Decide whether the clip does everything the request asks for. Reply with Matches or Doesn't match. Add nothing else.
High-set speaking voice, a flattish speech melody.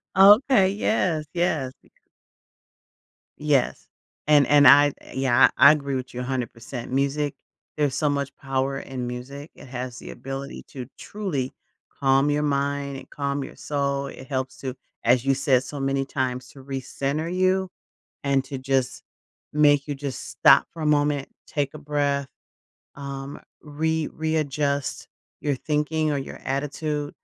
Doesn't match